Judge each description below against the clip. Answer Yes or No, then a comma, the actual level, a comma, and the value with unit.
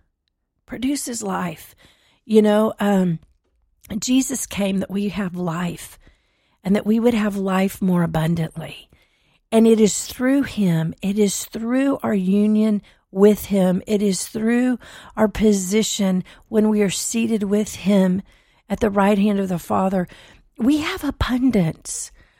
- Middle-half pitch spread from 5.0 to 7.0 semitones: No, average, 3.3 semitones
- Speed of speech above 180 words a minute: No, average, 140 wpm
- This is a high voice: Yes, high, 200 Hz